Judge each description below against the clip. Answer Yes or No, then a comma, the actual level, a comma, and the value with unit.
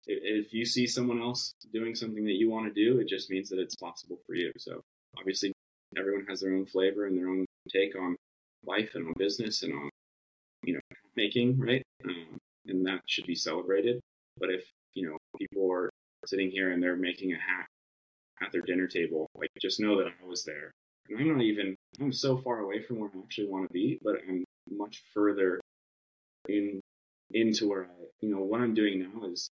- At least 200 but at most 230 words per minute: Yes, fast, 205 wpm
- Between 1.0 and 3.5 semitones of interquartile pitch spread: Yes, average, 3.0 semitones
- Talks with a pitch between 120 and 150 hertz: No, very low, 95 Hz